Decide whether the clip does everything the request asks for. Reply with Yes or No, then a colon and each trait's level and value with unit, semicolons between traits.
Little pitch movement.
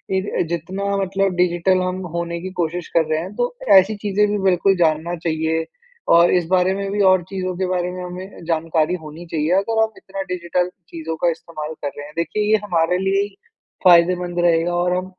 Yes: narrow, 2.3 semitones